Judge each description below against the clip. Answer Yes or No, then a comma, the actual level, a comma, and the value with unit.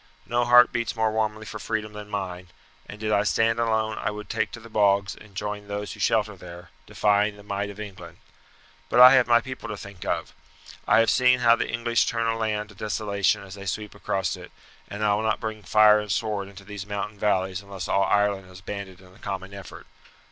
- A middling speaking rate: No, fast, 225 wpm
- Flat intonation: Yes, narrow, 1.8 semitones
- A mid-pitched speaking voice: No, low, 105 Hz